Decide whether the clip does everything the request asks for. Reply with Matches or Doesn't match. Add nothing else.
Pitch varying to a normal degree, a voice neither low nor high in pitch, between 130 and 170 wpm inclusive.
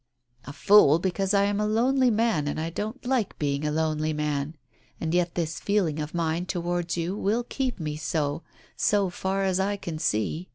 Doesn't match